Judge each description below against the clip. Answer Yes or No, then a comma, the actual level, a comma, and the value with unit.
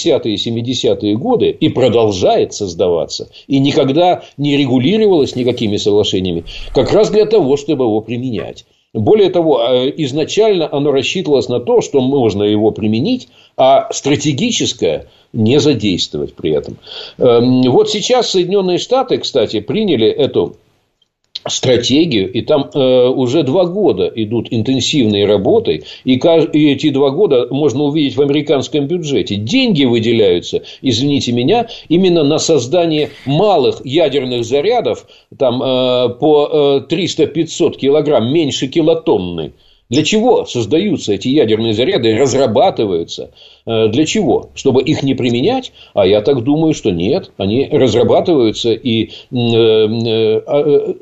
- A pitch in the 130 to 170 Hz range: Yes, medium, 140 Hz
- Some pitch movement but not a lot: No, wide, 6.1 semitones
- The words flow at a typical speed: Yes, average, 125 wpm